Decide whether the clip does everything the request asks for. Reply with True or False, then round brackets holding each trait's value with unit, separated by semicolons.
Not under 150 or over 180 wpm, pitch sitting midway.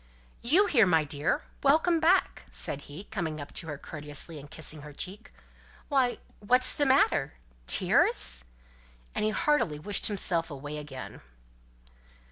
False (140 wpm; 165 Hz)